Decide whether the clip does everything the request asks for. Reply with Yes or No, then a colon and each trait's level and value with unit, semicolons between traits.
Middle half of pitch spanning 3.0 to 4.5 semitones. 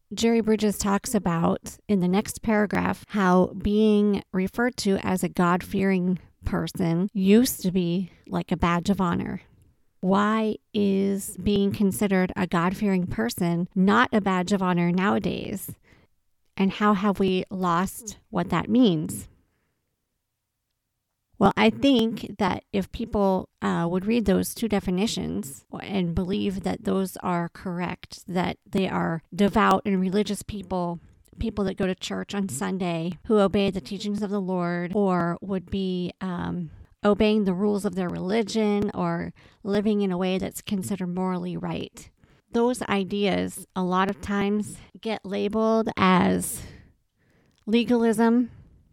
No: narrow, 2.6 semitones